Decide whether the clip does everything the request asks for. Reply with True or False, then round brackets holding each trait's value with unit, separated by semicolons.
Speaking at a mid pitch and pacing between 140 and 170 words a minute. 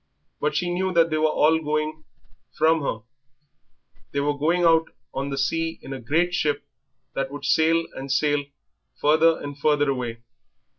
True (150 Hz; 165 wpm)